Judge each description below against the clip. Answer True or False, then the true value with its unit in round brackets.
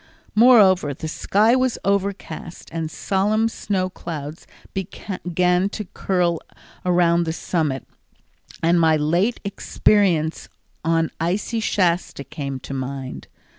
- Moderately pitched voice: True (175 Hz)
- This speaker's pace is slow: True (110 wpm)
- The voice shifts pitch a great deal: False (3.9 semitones)